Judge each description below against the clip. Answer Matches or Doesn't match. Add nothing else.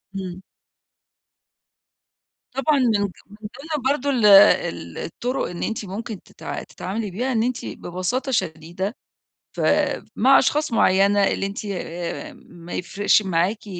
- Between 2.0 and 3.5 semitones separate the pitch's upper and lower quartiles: Doesn't match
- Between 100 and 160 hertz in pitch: Doesn't match